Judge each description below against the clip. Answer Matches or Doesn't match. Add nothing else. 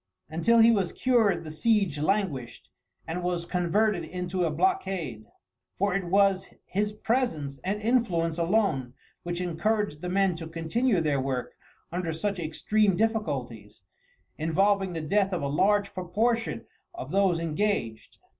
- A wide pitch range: Doesn't match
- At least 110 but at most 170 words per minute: Matches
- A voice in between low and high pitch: Matches